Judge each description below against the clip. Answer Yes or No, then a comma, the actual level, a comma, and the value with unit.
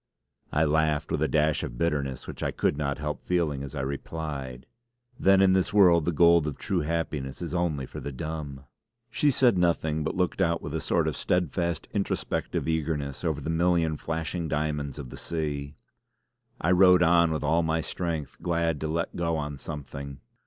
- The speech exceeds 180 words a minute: Yes, average, 190 wpm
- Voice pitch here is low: Yes, very low, 80 Hz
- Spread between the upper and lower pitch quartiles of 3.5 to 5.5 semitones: No, average, 2.7 semitones